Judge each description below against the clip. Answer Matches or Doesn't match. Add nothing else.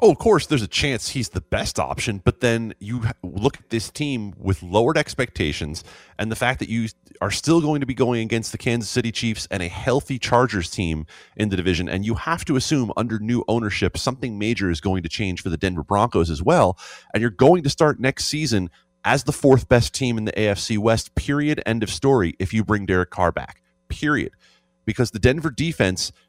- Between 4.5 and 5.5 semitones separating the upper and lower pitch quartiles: Matches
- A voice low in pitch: Matches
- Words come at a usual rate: Doesn't match